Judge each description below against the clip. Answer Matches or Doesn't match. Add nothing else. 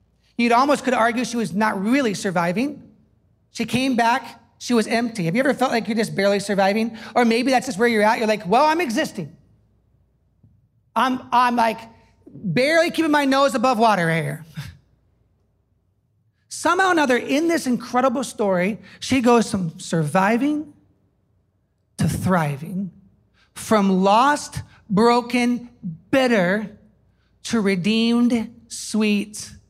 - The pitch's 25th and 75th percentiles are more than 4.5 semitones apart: Matches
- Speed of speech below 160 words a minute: Matches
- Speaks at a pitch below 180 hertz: Doesn't match